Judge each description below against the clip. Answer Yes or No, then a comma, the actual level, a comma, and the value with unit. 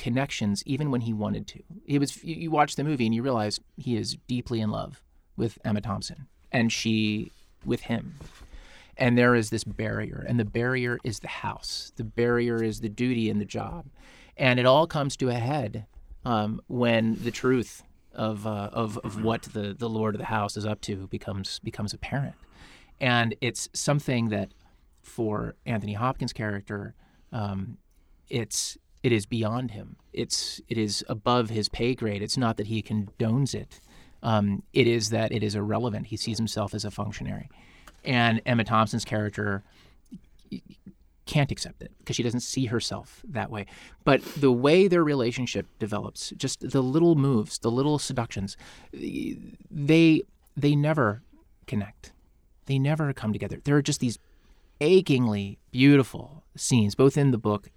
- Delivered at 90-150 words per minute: No, average, 165 wpm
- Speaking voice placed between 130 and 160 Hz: No, low, 115 Hz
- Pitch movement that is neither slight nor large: Yes, average, 3.6 semitones